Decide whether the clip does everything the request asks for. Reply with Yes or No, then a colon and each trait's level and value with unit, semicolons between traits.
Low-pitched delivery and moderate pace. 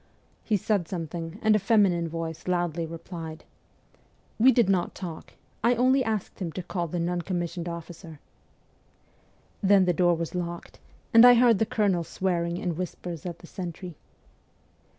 No: medium, 175 Hz; average, 160 wpm